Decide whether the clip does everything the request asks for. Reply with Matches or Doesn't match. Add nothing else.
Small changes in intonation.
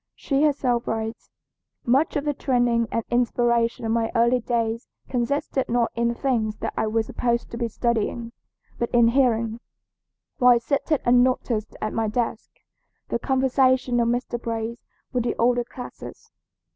Matches